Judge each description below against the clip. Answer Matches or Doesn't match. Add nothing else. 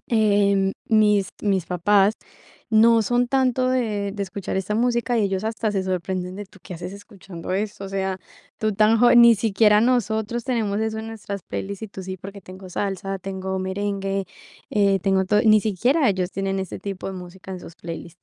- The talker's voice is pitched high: Matches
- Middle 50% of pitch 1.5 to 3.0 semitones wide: Matches